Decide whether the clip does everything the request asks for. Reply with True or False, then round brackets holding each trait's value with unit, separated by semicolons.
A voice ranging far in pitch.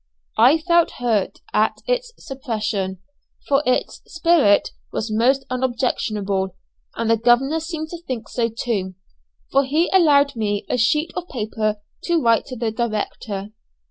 True (5.8 semitones)